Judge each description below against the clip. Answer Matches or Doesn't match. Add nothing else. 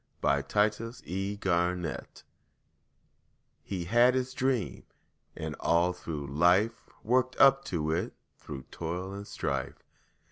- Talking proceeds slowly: Matches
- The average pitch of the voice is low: Matches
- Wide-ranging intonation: Matches